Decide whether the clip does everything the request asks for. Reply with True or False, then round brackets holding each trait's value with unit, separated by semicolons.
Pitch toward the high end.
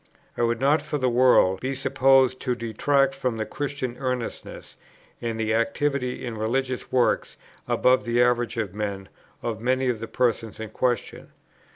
False (125 Hz)